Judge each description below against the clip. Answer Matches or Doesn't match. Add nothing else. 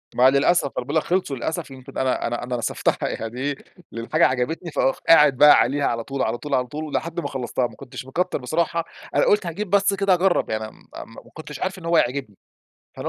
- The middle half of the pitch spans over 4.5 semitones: Matches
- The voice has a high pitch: Doesn't match